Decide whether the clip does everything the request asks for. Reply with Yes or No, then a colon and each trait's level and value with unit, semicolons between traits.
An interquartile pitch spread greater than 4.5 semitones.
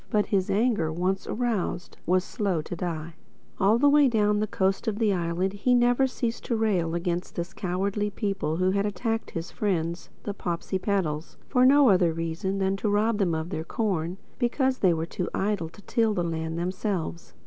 No: average, 3.9 semitones